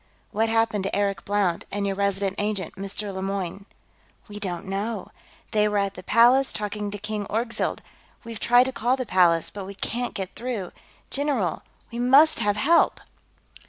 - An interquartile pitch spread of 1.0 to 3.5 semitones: Yes, average, 2.9 semitones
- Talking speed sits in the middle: Yes, average, 170 wpm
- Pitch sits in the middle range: No, high, 205 Hz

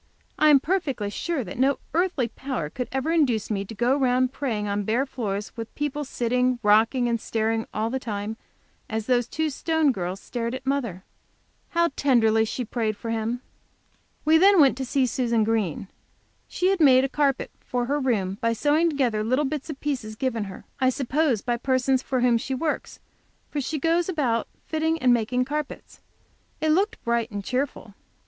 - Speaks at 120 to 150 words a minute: No, average, 185 wpm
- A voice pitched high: Yes, very high, 255 Hz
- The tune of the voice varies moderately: Yes, average, 4.3 semitones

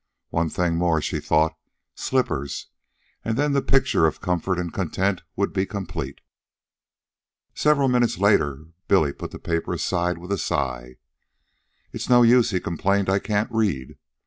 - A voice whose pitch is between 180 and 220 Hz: No, very low, 90 Hz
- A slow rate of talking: No, average, 150 wpm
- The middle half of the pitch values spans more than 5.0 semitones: Yes, wide, 5.4 semitones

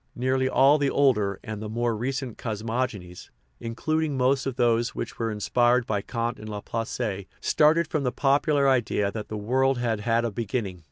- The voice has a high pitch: No, low, 120 Hz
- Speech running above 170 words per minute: Yes, average, 180 wpm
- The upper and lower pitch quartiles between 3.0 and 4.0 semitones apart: Yes, average, 3.6 semitones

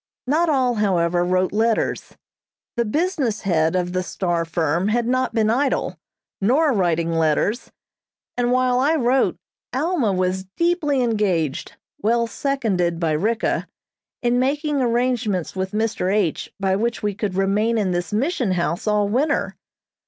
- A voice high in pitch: Yes, high, 215 Hz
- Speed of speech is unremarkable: Yes, average, 145 wpm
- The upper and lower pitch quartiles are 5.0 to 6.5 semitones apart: Yes, wide, 5.6 semitones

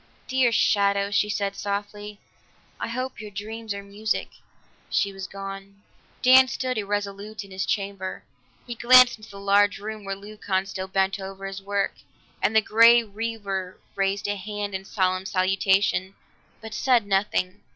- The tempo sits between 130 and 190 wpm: Yes, average, 160 wpm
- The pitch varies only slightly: Yes, narrow, 1.7 semitones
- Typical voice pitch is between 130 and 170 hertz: No, high, 200 Hz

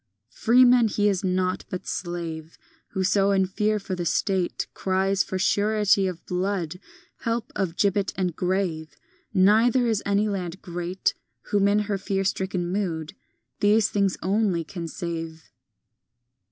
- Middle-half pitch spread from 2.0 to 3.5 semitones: Yes, narrow, 2.5 semitones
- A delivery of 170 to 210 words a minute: No, average, 140 wpm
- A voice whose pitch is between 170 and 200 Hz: Yes, high, 190 Hz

